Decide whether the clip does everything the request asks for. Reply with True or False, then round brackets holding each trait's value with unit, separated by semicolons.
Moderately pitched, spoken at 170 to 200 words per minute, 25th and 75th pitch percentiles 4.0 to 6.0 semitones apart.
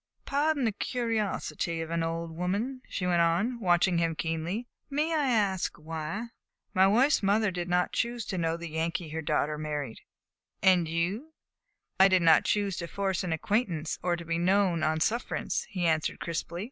True (180 Hz; 175 wpm; 4.3 semitones)